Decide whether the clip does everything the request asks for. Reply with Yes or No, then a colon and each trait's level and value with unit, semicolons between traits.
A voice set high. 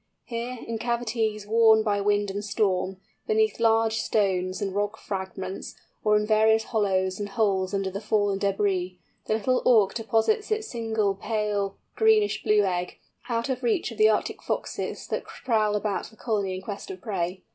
Yes: high, 210 Hz